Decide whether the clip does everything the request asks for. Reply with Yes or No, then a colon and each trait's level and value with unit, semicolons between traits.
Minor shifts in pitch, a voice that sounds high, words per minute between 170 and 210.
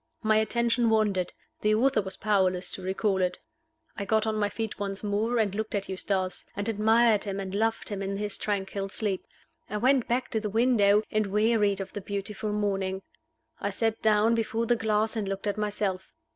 Yes: narrow, 2.0 semitones; high, 210 Hz; average, 195 wpm